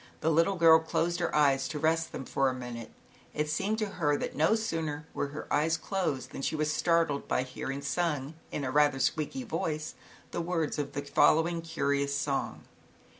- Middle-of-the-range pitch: Yes, medium, 150 Hz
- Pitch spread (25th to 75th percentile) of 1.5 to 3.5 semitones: Yes, average, 2.8 semitones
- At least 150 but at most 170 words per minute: No, average, 190 wpm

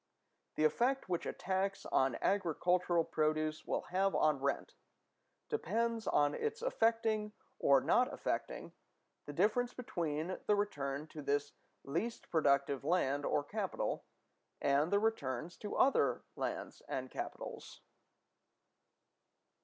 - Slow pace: Yes, slow, 120 wpm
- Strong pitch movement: Yes, wide, 7.1 semitones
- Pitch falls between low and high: Yes, medium, 175 Hz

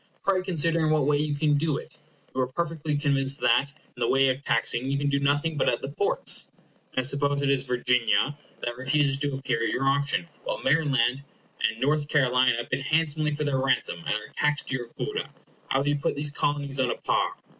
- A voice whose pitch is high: No, medium, 140 Hz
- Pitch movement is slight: Yes, narrow, 2.3 semitones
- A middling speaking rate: No, fast, 220 wpm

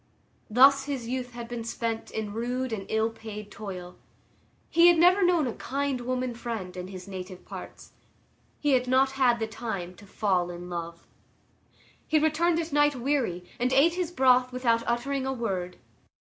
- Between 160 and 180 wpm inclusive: Yes, average, 170 wpm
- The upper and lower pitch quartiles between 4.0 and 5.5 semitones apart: Yes, average, 4.8 semitones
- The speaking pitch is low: No, high, 240 Hz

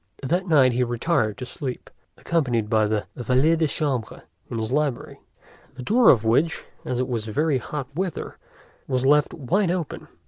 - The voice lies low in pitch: Yes, low, 130 Hz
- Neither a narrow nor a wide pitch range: Yes, average, 5.0 semitones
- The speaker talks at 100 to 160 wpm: No, average, 170 wpm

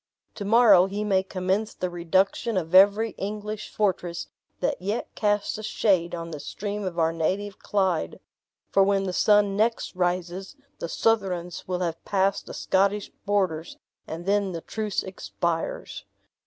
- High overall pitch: Yes, high, 195 Hz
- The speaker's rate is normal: Yes, average, 155 wpm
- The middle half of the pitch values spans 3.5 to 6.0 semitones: No, average, 2.7 semitones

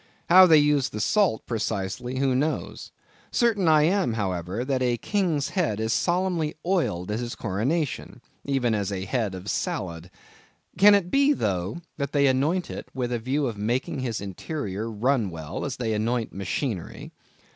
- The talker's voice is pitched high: No, low, 125 Hz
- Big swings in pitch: Yes, wide, 6.8 semitones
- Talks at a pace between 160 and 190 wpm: Yes, average, 165 wpm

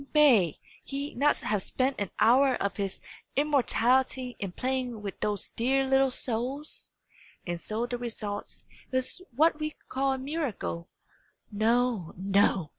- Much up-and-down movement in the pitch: No, average, 4.7 semitones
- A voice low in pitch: No, high, 245 Hz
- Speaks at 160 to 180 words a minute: No, slow, 135 wpm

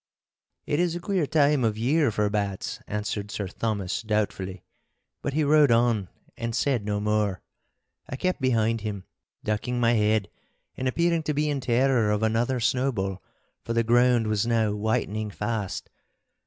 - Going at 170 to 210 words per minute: No, average, 160 wpm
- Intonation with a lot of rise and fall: No, average, 3.9 semitones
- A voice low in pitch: Yes, low, 115 Hz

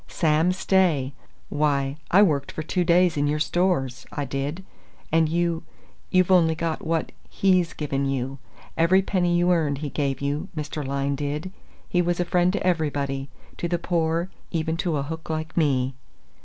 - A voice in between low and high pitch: Yes, medium, 160 Hz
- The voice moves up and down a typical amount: Yes, average, 3.6 semitones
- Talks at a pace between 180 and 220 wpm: No, average, 170 wpm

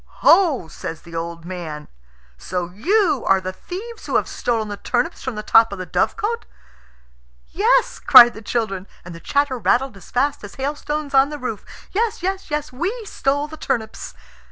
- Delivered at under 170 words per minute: No, average, 180 wpm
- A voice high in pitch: Yes, high, 245 Hz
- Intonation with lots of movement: Yes, wide, 7.9 semitones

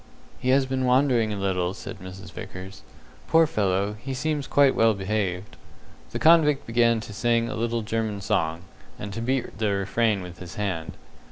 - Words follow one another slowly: No, average, 175 wpm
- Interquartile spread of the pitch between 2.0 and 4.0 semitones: No, average, 4.5 semitones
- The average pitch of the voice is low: Yes, low, 110 Hz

